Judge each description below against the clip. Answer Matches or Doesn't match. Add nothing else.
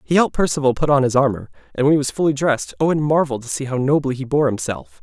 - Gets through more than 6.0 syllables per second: Matches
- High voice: Doesn't match